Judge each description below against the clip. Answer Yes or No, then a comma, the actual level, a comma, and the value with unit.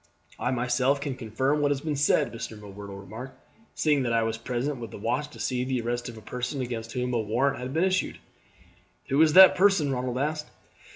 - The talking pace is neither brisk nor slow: No, fast, 215 wpm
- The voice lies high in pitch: No, low, 125 Hz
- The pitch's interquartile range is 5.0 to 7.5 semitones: No, average, 3.6 semitones